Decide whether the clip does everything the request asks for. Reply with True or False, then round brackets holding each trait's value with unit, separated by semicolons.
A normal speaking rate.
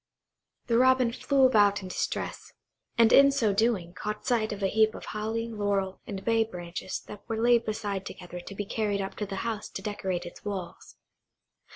True (190 wpm)